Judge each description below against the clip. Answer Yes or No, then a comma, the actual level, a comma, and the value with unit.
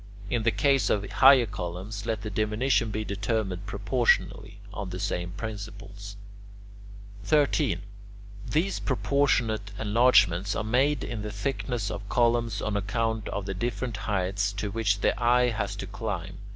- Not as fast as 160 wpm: Yes, average, 145 wpm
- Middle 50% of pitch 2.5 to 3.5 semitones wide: Yes, average, 3.0 semitones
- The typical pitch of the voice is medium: No, low, 105 Hz